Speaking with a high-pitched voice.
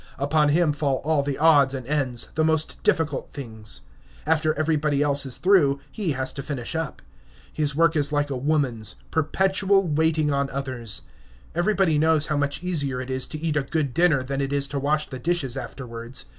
No: medium, 145 Hz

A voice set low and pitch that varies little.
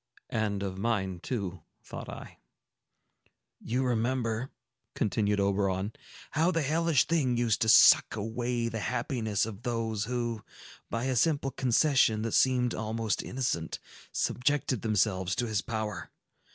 No: low, 115 Hz; average, 3.3 semitones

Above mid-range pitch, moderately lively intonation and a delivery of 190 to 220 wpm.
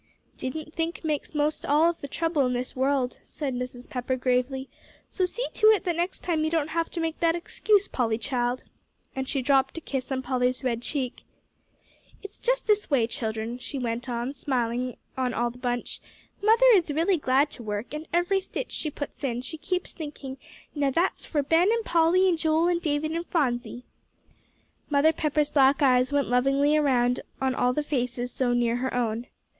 Yes: very high, 280 Hz; average, 4.5 semitones; average, 195 wpm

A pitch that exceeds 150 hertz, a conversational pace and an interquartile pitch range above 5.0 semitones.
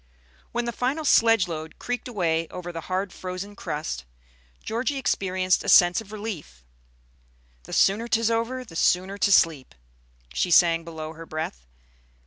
Yes: medium, 185 Hz; average, 150 wpm; wide, 5.5 semitones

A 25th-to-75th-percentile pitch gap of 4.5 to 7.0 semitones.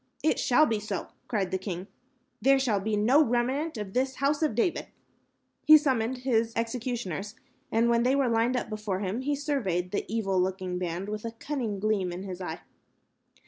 Yes: average, 4.9 semitones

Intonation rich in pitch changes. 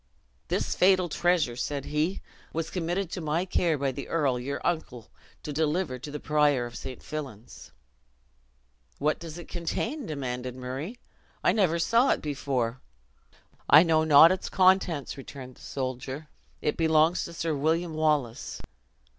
No: average, 4.0 semitones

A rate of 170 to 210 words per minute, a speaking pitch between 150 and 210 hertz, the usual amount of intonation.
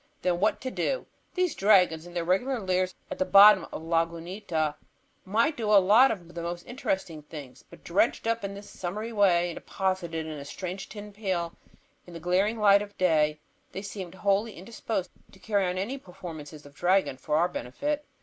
Yes: average, 190 wpm; medium, 185 Hz; average, 3.5 semitones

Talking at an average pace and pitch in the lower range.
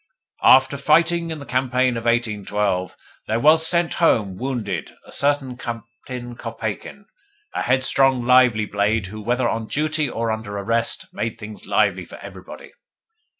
Yes: average, 145 wpm; low, 120 Hz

